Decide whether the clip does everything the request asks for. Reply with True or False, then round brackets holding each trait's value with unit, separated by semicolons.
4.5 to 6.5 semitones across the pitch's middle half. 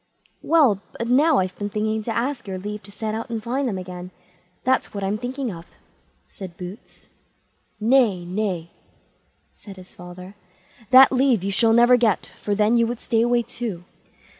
False (4.1 semitones)